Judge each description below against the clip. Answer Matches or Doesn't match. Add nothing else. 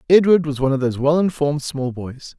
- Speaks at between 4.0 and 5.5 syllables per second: Doesn't match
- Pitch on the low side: Doesn't match